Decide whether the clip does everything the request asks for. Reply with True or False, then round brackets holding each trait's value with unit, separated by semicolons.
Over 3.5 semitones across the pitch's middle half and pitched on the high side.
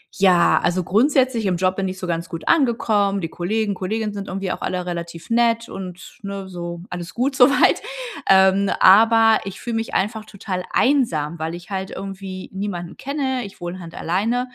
True (3.9 semitones; 195 Hz)